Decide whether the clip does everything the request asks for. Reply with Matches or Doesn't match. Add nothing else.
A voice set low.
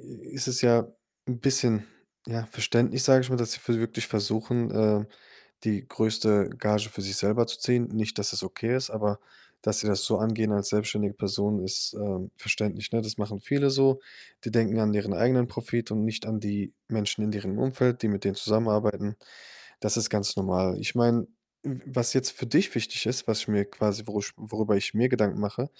Matches